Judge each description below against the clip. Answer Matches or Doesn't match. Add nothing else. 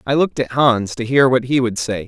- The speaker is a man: Matches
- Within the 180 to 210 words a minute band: Doesn't match